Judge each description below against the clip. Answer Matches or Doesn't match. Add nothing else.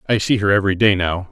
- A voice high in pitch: Doesn't match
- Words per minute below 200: Doesn't match